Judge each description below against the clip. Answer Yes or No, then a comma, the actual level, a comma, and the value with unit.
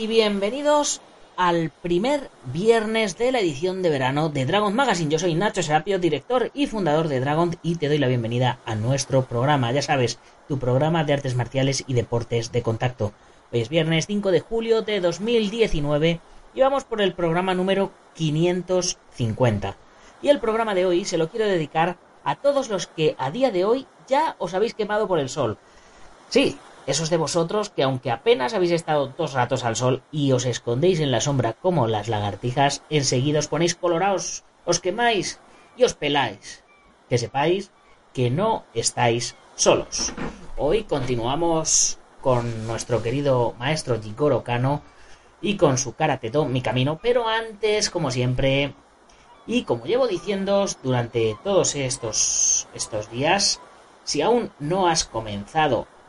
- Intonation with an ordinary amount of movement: No, wide, 7.4 semitones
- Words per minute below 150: No, average, 160 wpm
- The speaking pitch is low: No, medium, 155 Hz